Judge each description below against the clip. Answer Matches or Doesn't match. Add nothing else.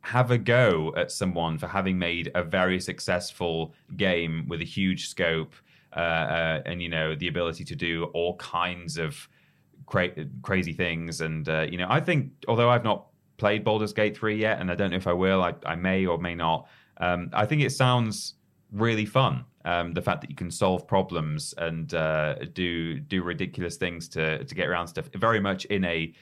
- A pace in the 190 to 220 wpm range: Matches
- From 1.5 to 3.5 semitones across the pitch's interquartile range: Doesn't match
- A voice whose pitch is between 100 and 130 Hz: Doesn't match